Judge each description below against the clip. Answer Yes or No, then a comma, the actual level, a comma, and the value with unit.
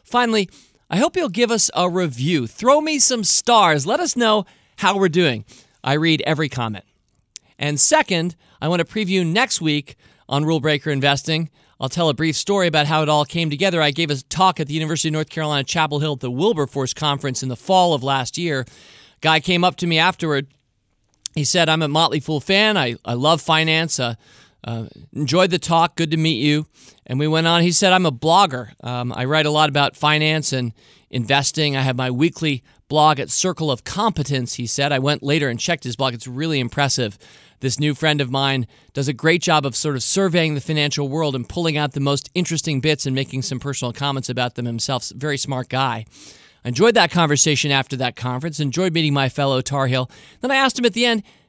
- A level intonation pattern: No, average, 3.8 semitones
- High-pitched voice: No, medium, 150 Hz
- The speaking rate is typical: No, fast, 215 wpm